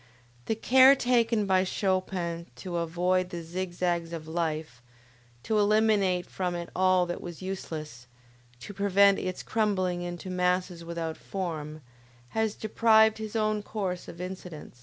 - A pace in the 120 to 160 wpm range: Yes, average, 140 wpm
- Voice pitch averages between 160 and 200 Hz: Yes, medium, 185 Hz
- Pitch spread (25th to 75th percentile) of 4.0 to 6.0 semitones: No, average, 3.2 semitones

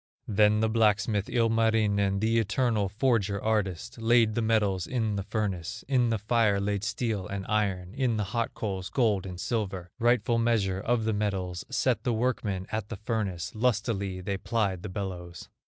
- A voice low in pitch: Yes, low, 105 Hz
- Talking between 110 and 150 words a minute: No, average, 170 wpm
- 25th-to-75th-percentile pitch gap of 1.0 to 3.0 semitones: Yes, average, 2.7 semitones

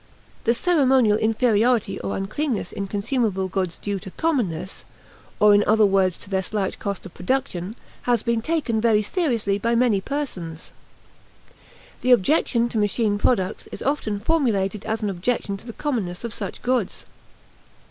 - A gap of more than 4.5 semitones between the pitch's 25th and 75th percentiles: No, average, 4.1 semitones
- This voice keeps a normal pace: Yes, average, 155 wpm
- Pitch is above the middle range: Yes, high, 215 Hz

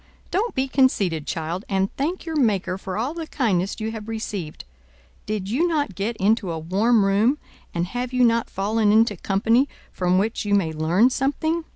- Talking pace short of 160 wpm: No, average, 185 wpm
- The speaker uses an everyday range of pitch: Yes, average, 4.9 semitones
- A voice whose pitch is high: Yes, high, 215 Hz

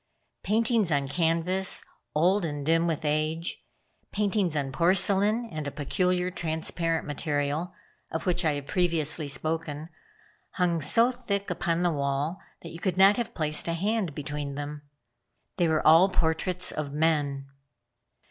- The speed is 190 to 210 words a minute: No, average, 140 wpm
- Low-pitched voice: No, medium, 165 Hz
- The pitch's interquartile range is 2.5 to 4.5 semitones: Yes, average, 3.5 semitones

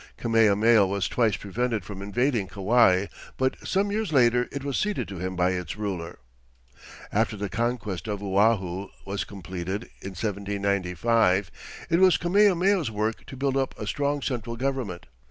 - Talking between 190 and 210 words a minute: No, average, 155 wpm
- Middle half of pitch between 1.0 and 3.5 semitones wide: No, average, 5.1 semitones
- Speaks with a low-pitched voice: Yes, low, 110 Hz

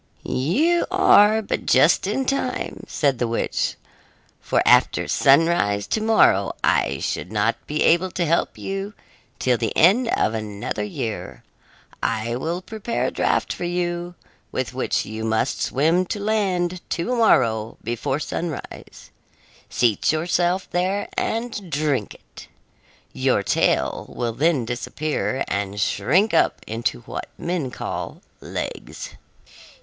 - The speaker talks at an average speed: No, slow, 130 wpm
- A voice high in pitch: No, medium, 160 Hz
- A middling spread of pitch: No, wide, 8.3 semitones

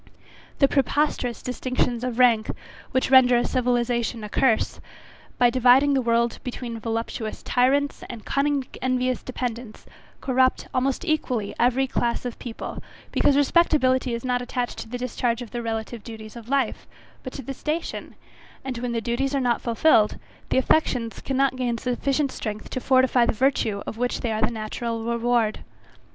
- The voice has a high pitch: Yes, high, 245 Hz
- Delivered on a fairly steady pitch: Yes, narrow, 2.0 semitones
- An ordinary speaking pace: Yes, average, 160 wpm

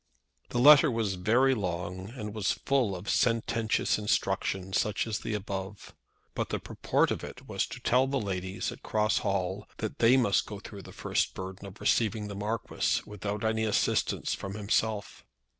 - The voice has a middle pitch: No, low, 105 Hz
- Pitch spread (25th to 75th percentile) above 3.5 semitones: No, average, 2.7 semitones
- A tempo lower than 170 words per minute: No, average, 175 wpm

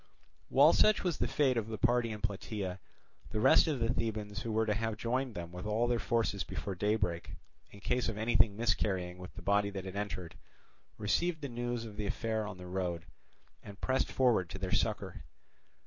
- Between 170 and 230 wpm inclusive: Yes, average, 200 wpm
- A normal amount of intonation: Yes, average, 3.2 semitones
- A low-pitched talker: Yes, low, 105 Hz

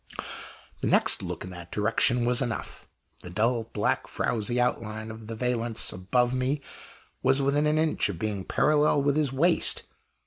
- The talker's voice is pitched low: Yes, low, 120 Hz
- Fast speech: No, average, 165 wpm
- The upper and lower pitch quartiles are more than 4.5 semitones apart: No, average, 4.1 semitones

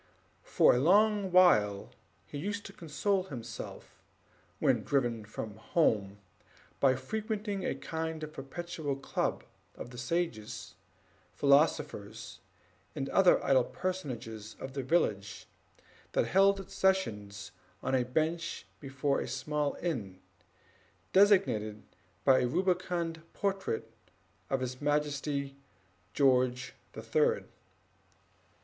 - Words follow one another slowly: Yes, slow, 110 wpm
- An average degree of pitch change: No, wide, 6.7 semitones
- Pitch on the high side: No, medium, 140 Hz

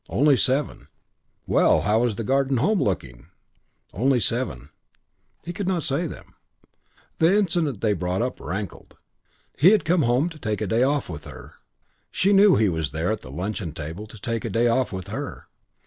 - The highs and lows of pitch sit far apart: Yes, wide, 7.6 semitones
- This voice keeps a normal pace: Yes, average, 185 wpm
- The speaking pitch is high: No, low, 115 Hz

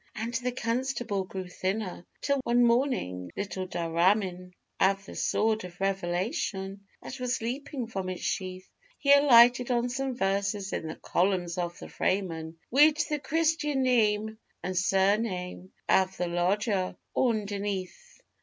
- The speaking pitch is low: No, high, 200 Hz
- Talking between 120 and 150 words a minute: Yes, average, 140 wpm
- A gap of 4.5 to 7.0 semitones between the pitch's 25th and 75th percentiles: Yes, average, 4.8 semitones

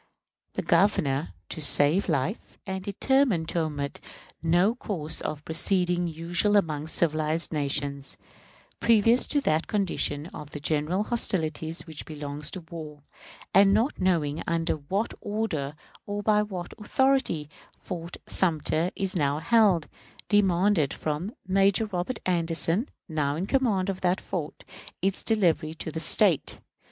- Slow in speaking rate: Yes, slow, 130 wpm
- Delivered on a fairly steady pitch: No, average, 4.5 semitones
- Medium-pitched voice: Yes, medium, 175 Hz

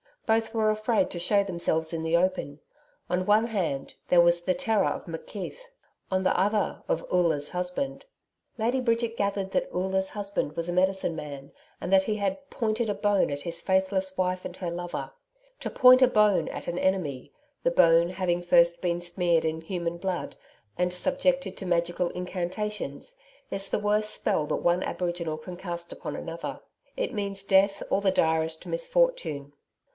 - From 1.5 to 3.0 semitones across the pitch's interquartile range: No, average, 3.5 semitones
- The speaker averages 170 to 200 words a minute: Yes, average, 175 wpm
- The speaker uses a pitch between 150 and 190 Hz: Yes, medium, 185 Hz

